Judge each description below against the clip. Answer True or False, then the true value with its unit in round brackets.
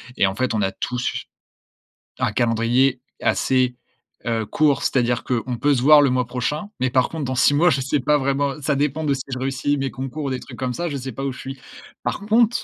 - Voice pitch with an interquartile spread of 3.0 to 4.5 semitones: False (2.6 semitones)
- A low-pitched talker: True (130 Hz)